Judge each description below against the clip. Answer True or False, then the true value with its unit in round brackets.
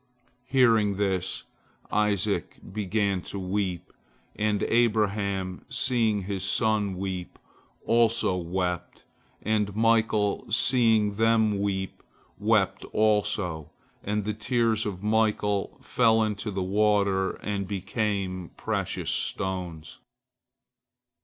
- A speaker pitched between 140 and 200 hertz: False (105 Hz)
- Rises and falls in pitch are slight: True (2.3 semitones)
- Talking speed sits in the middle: False (95 wpm)